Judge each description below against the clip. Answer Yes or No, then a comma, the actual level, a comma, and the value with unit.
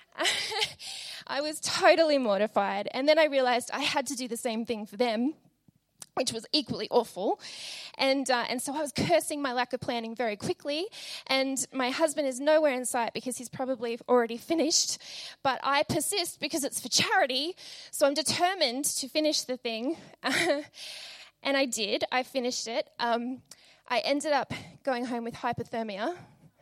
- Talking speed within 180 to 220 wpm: No, average, 165 wpm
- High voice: Yes, very high, 265 Hz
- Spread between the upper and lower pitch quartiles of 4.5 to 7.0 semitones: No, average, 4.0 semitones